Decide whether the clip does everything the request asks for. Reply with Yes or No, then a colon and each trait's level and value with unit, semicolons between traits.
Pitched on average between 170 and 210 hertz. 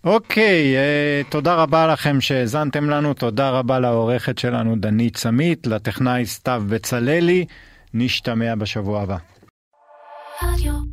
No: low, 125 Hz